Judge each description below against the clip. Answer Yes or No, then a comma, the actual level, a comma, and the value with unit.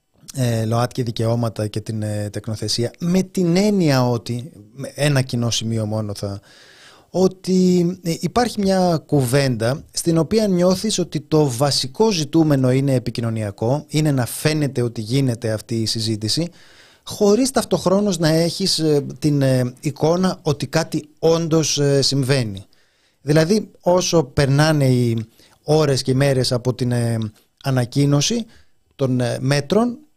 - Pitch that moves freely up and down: Yes, wide, 5.8 semitones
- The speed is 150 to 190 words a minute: No, slow, 115 wpm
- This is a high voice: No, medium, 140 Hz